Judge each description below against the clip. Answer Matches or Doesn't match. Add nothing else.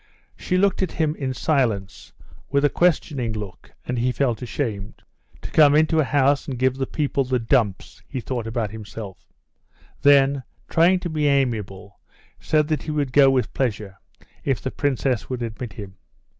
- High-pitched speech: Doesn't match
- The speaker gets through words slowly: Doesn't match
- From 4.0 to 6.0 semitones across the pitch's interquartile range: Matches